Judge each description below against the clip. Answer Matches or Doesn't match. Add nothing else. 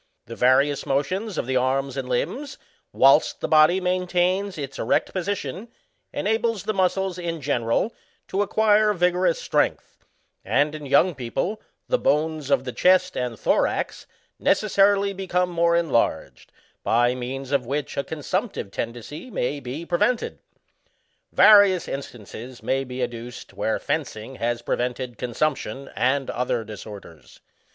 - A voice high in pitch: Doesn't match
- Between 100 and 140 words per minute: Matches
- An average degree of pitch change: Doesn't match